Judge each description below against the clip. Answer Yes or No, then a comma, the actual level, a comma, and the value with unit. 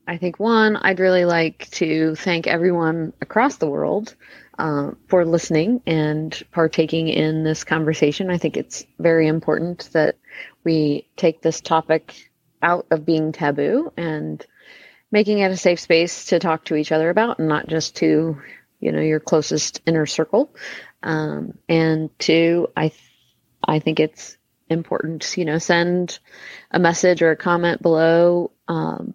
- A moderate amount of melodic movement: No, narrow, 1.8 semitones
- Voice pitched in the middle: Yes, medium, 165 Hz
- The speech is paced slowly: No, average, 155 wpm